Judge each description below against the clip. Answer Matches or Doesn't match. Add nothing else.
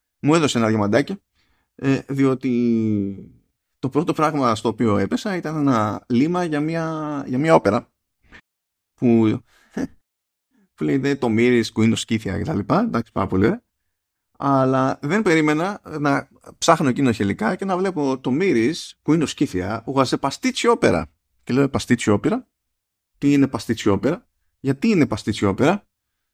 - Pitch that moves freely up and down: Matches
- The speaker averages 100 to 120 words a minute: Doesn't match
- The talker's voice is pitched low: Matches